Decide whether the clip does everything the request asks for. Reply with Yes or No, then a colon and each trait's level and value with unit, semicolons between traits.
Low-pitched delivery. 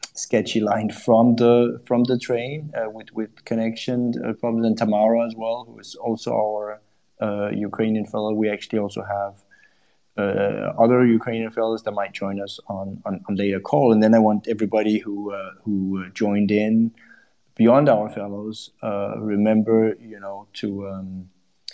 Yes: low, 110 Hz